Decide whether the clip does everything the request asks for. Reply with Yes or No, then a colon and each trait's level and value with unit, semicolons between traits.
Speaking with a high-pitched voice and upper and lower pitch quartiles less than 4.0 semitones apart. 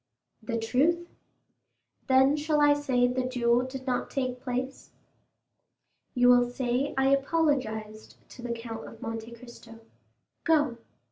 Yes: very high, 250 Hz; narrow, 2.6 semitones